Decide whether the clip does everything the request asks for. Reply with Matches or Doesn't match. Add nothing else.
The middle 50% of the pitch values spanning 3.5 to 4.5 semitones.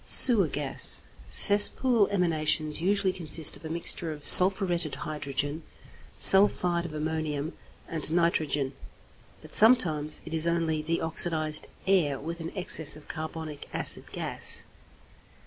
Doesn't match